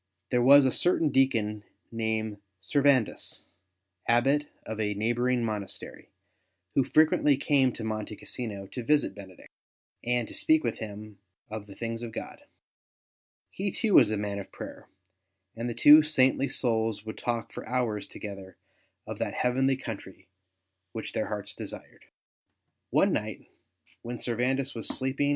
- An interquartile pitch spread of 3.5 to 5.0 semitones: Yes, average, 3.8 semitones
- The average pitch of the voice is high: No, low, 120 Hz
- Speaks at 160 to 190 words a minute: No, average, 150 wpm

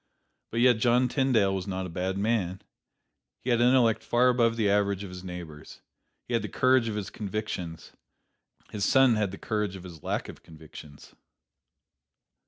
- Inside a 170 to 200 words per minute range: Yes, average, 175 wpm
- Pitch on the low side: Yes, low, 105 Hz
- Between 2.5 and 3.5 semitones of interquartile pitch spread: No, average, 4.3 semitones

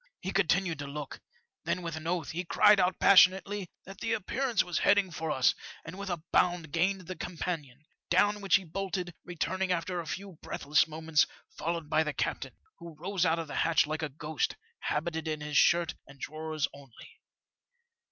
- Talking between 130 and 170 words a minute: No, average, 185 wpm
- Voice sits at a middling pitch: Yes, medium, 170 Hz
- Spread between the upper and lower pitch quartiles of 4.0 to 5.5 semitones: No, average, 3.2 semitones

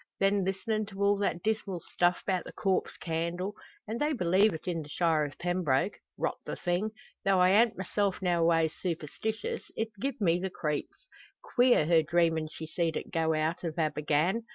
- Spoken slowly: No, average, 180 wpm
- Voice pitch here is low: No, medium, 180 Hz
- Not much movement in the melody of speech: No, average, 3.8 semitones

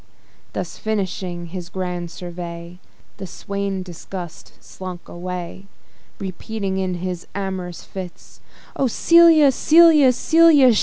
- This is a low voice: No, medium, 185 Hz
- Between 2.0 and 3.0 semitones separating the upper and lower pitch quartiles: No, average, 3.7 semitones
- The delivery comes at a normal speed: No, slow, 105 wpm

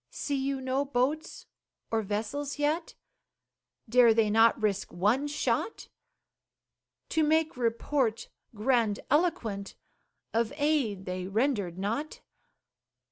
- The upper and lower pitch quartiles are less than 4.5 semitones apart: No, average, 5.3 semitones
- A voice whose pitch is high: Yes, high, 245 Hz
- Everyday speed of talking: No, slow, 100 wpm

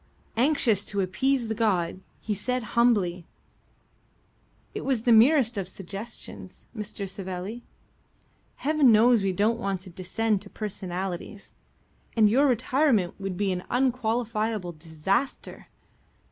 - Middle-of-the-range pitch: No, high, 210 Hz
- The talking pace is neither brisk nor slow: No, slow, 120 wpm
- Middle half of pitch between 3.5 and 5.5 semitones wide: Yes, average, 4.1 semitones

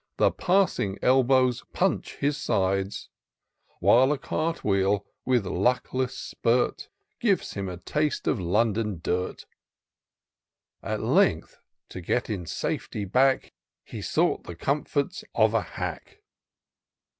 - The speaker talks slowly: Yes, slow, 120 wpm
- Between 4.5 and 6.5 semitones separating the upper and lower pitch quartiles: Yes, wide, 5.4 semitones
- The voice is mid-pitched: No, low, 115 Hz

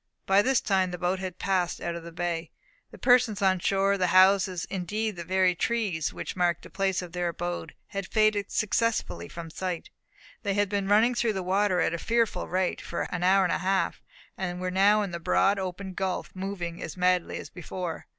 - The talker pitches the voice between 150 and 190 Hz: Yes, medium, 185 Hz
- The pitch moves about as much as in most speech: No, narrow, 2.1 semitones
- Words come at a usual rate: No, fast, 210 wpm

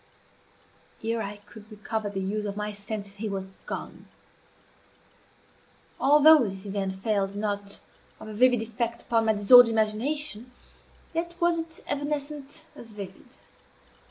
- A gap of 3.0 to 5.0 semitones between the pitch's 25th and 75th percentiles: Yes, average, 4.7 semitones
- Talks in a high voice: Yes, high, 220 Hz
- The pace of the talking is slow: Yes, slow, 130 wpm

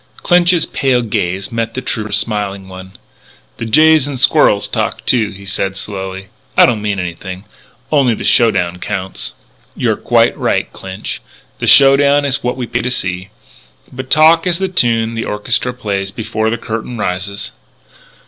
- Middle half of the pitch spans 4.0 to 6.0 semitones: Yes, average, 5.0 semitones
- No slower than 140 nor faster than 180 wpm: Yes, average, 165 wpm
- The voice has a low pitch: Yes, low, 110 Hz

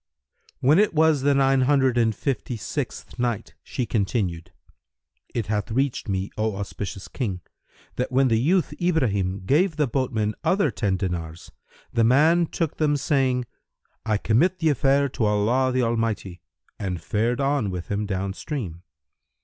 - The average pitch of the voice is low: Yes, low, 120 Hz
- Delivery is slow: No, average, 155 wpm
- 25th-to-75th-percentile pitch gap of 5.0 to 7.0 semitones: Yes, wide, 5.6 semitones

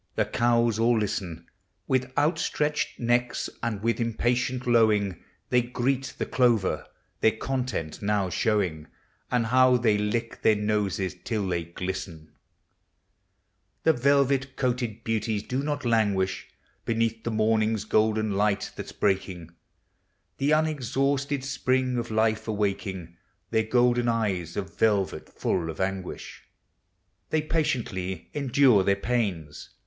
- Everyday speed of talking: No, slow, 125 wpm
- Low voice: Yes, low, 110 Hz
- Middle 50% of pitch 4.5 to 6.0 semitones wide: No, average, 4.0 semitones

